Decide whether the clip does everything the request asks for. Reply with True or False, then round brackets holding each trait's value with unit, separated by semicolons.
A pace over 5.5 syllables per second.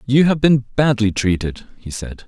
False (4.5 syllables/s)